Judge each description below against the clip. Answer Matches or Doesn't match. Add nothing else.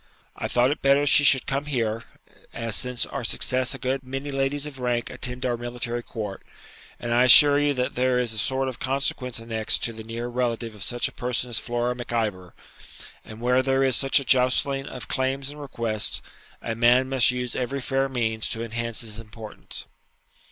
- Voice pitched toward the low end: Matches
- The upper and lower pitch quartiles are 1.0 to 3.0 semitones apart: Matches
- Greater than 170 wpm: Matches